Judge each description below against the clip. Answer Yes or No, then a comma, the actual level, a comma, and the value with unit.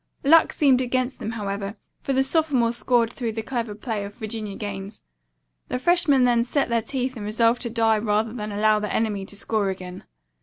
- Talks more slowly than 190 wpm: No, average, 195 wpm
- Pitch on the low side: No, high, 225 Hz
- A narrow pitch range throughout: No, average, 3.1 semitones